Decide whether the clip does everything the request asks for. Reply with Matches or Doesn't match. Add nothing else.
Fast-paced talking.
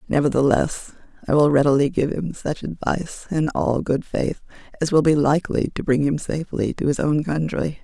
Doesn't match